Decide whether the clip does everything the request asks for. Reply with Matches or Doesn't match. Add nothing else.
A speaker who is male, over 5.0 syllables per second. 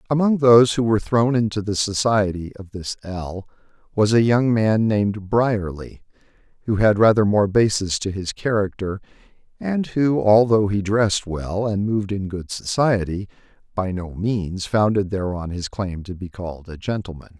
Doesn't match